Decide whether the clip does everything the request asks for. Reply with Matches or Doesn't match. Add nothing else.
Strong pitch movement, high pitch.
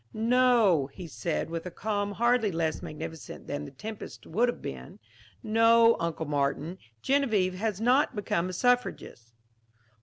Matches